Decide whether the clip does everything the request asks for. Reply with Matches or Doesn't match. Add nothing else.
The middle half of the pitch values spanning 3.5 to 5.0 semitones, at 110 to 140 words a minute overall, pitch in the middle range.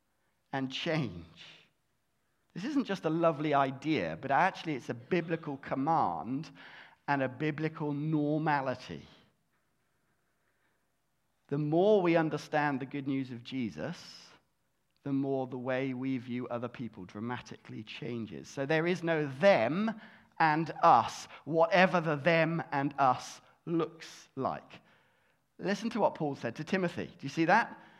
Matches